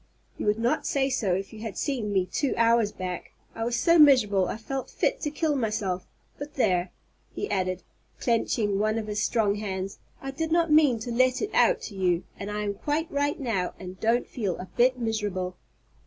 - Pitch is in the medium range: No, high, 225 Hz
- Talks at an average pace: No, fast, 210 wpm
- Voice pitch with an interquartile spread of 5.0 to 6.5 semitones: Yes, wide, 5.4 semitones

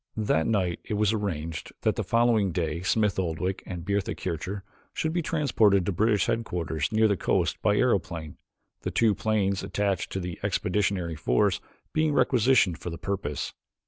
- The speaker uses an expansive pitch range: No, average, 4.1 semitones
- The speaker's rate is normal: Yes, average, 165 wpm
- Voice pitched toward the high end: No, low, 100 Hz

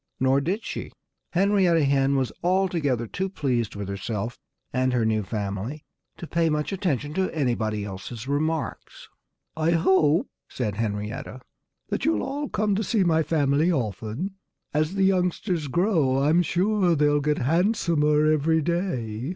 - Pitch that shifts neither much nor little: No, wide, 6.3 semitones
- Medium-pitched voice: Yes, medium, 150 Hz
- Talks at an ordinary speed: Yes, average, 145 wpm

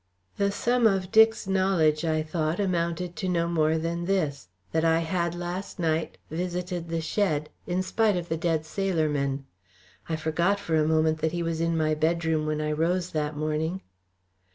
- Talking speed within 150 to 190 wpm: Yes, average, 180 wpm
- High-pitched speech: No, medium, 165 Hz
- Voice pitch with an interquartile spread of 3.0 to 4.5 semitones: No, narrow, 2.5 semitones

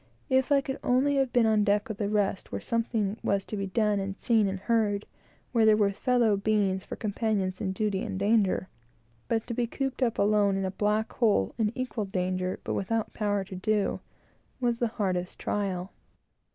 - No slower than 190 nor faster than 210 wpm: Yes, average, 200 wpm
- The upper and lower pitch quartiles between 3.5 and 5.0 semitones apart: No, average, 2.8 semitones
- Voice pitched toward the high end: Yes, high, 210 Hz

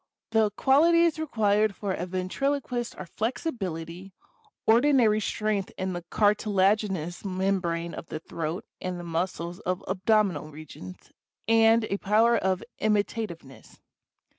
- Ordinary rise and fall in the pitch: Yes, average, 4.1 semitones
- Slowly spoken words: Yes, slow, 120 wpm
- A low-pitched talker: No, high, 200 Hz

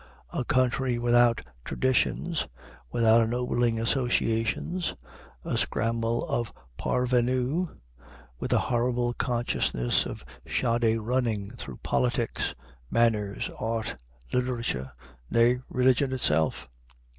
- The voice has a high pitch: No, low, 120 Hz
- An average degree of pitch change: No, narrow, 1.8 semitones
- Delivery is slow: Yes, slow, 90 wpm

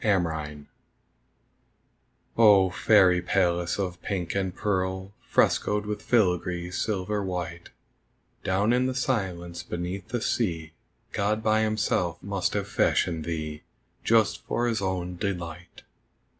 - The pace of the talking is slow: Yes, slow, 125 wpm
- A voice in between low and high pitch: No, very low, 95 Hz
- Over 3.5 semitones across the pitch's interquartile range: No, average, 3.2 semitones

